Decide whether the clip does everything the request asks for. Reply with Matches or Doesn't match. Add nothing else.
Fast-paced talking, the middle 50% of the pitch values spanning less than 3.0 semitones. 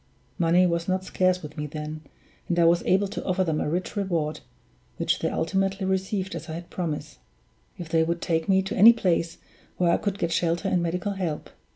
Matches